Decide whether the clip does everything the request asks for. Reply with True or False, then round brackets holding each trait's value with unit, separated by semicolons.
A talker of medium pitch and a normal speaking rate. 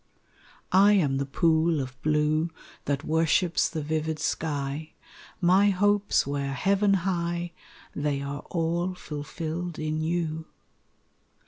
False (160 Hz; 115 wpm)